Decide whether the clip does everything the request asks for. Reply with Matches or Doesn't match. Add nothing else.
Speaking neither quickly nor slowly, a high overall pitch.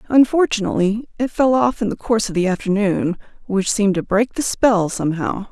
Matches